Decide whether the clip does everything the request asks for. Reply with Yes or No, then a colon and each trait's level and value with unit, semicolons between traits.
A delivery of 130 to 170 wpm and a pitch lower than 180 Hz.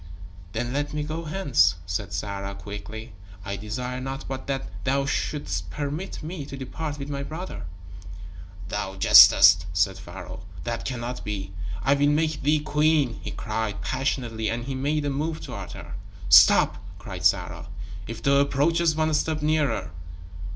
Yes: average, 155 wpm; low, 135 Hz